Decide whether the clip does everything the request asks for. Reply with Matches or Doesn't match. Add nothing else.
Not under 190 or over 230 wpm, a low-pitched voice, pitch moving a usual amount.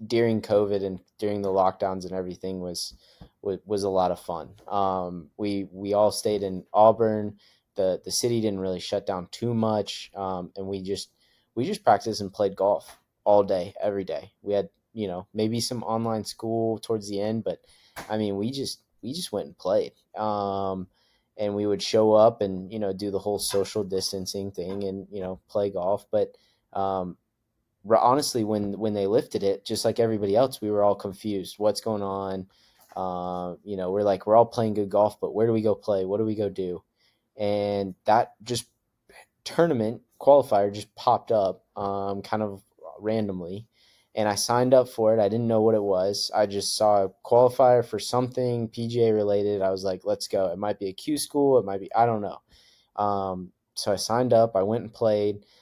Doesn't match